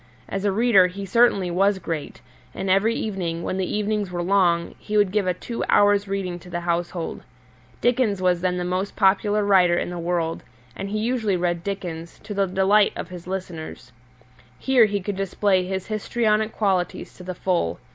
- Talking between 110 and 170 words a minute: No, average, 185 wpm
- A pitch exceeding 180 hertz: Yes, high, 190 Hz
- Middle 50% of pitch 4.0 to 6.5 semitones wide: No, narrow, 2.5 semitones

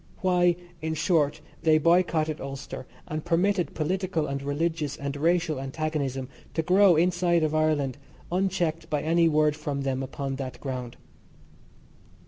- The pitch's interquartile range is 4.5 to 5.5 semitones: No, average, 3.4 semitones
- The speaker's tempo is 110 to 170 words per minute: Yes, slow, 135 wpm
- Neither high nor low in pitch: Yes, medium, 155 Hz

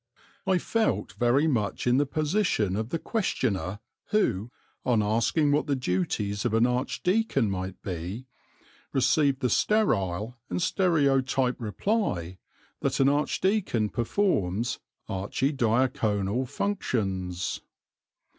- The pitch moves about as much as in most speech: No, wide, 6.6 semitones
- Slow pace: Yes, slow, 110 wpm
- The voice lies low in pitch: Yes, low, 125 Hz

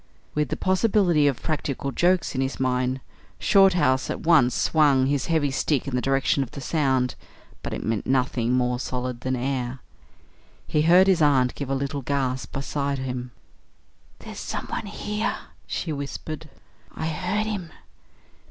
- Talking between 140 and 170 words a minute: Yes, average, 155 wpm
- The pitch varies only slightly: No, average, 3.7 semitones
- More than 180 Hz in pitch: No, medium, 140 Hz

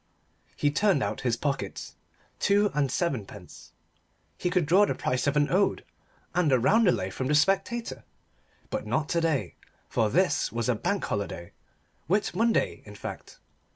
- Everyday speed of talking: Yes, average, 160 wpm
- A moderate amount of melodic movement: No, wide, 7.2 semitones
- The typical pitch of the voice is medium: Yes, medium, 150 Hz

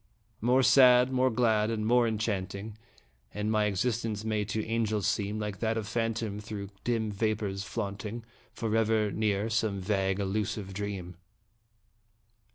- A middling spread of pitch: No, narrow, 1.8 semitones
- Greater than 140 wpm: No, slow, 135 wpm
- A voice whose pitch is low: Yes, low, 110 Hz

